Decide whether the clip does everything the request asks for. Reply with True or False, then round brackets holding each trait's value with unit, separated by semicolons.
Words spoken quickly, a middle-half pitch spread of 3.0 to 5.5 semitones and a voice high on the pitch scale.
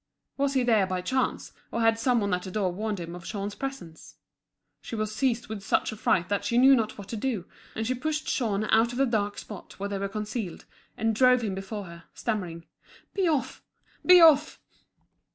True (215 wpm; 4.2 semitones; 220 Hz)